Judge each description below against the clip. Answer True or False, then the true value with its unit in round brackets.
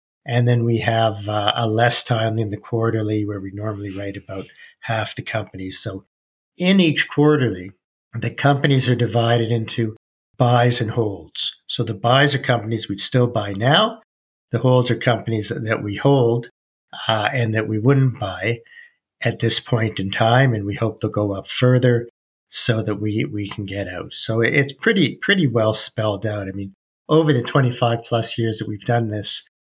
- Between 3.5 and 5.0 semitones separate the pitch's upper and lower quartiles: False (2.6 semitones)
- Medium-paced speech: True (180 wpm)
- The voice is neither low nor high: False (115 Hz)